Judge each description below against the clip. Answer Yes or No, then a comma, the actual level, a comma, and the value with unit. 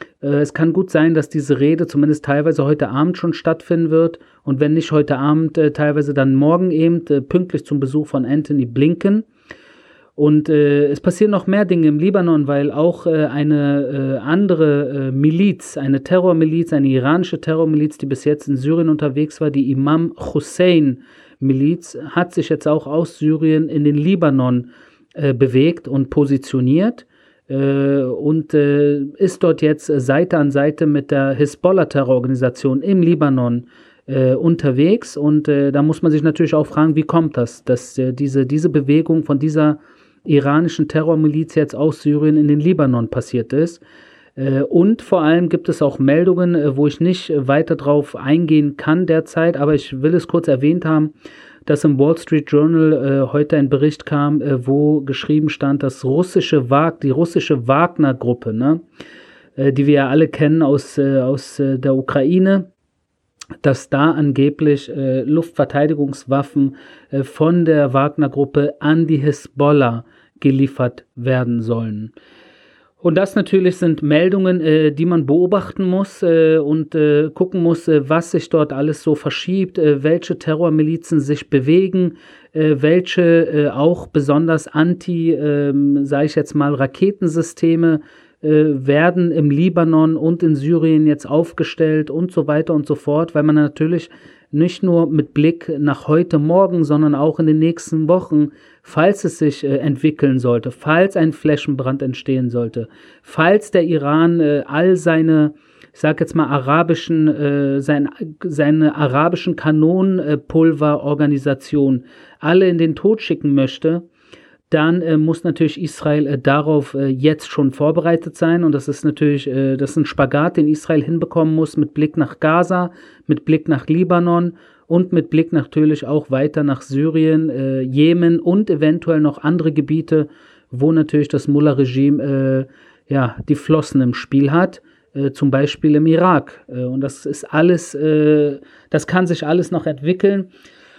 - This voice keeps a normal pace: Yes, average, 155 wpm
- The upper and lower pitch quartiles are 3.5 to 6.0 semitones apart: No, narrow, 2.5 semitones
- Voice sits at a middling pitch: Yes, medium, 150 Hz